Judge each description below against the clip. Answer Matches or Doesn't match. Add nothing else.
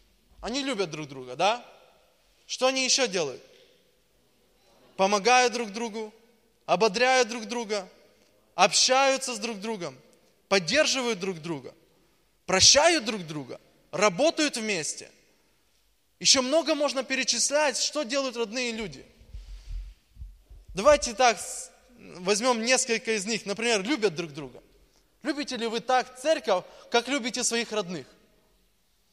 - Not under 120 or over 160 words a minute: Doesn't match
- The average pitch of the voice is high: Matches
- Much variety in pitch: Doesn't match